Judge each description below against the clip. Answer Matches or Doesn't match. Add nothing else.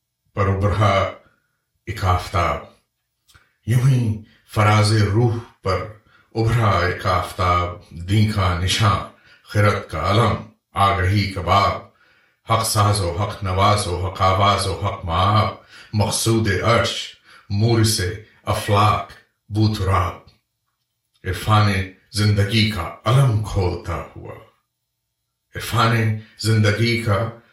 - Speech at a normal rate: Doesn't match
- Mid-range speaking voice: Doesn't match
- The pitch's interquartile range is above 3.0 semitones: Doesn't match